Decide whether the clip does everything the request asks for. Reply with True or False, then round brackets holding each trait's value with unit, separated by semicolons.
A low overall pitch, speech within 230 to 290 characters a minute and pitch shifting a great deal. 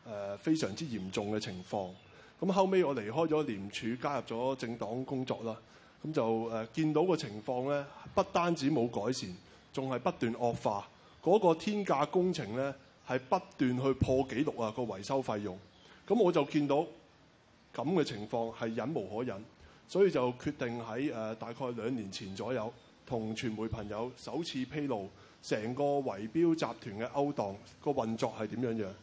False (125 Hz; 260 characters per minute; 4.8 semitones)